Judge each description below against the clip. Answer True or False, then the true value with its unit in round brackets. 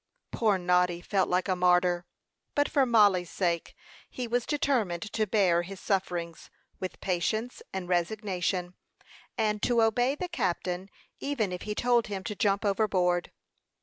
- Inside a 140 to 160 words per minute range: True (150 wpm)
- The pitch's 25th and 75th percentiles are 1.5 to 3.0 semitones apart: False (3.8 semitones)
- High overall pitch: True (195 Hz)